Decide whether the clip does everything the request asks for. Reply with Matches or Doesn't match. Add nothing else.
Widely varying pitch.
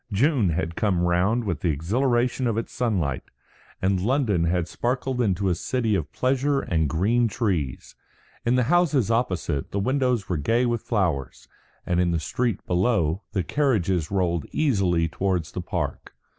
Matches